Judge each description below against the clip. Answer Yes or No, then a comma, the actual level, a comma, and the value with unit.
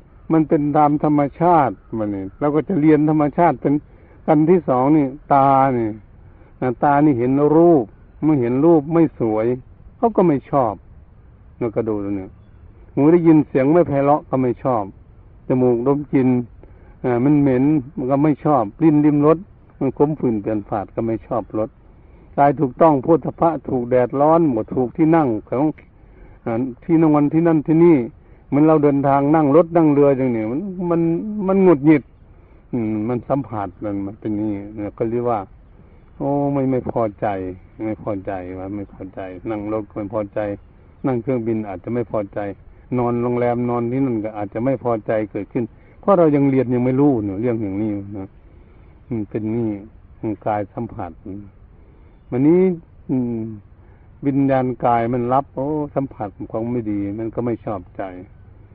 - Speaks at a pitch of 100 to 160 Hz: Yes, low, 120 Hz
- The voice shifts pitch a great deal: Yes, wide, 5.9 semitones